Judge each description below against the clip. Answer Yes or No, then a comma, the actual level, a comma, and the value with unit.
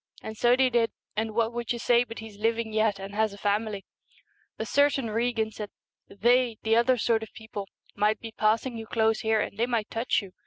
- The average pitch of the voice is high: Yes, high, 225 Hz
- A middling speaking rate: No, fast, 225 wpm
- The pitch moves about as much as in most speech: No, narrow, 1.7 semitones